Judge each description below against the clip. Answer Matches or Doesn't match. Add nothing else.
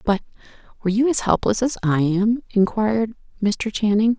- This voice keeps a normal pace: Matches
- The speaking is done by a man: Doesn't match